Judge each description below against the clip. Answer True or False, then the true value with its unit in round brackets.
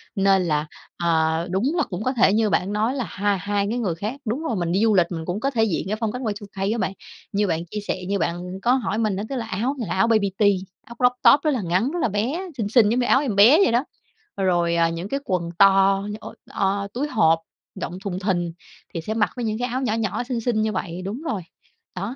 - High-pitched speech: True (205 Hz)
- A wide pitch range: False (4.3 semitones)